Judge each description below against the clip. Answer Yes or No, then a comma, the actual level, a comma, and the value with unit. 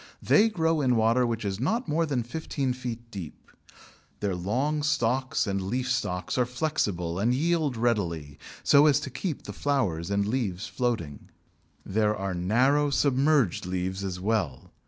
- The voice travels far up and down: Yes, wide, 6.5 semitones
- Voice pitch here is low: Yes, low, 120 Hz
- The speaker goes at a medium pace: Yes, average, 155 wpm